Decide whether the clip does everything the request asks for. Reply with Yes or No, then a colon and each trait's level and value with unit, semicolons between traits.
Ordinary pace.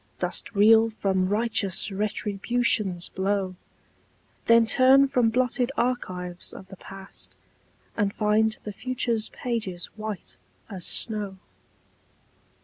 No: slow, 105 wpm